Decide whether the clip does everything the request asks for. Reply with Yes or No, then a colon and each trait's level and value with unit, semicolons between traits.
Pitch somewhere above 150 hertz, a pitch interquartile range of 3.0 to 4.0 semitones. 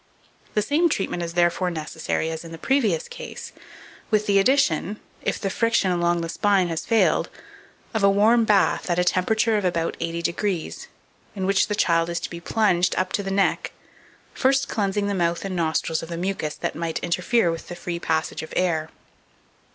Yes: medium, 185 Hz; average, 3.6 semitones